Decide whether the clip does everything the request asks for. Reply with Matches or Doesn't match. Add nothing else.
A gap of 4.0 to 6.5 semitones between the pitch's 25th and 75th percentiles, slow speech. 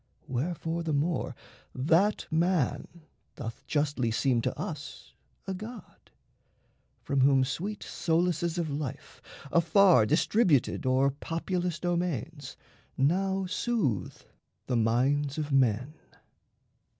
Matches